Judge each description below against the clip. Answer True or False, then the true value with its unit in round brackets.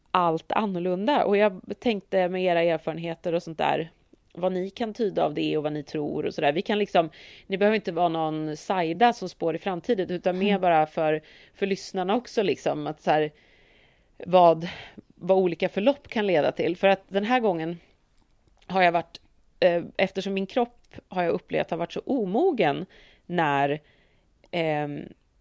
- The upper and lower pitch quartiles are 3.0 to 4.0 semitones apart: True (3.4 semitones)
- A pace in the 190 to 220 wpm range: False (175 wpm)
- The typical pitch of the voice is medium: True (180 Hz)